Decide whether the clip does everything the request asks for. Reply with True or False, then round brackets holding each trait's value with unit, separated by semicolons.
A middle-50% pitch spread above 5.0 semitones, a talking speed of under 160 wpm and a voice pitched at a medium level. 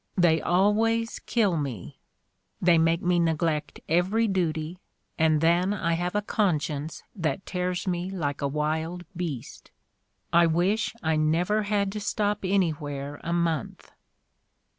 False (3.4 semitones; 140 wpm; 175 Hz)